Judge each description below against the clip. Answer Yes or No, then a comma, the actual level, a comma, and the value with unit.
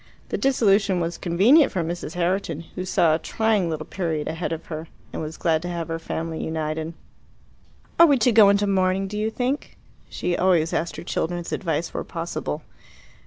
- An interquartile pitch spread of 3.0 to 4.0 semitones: Yes, average, 3.5 semitones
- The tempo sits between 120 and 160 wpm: No, average, 185 wpm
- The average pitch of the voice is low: No, medium, 175 Hz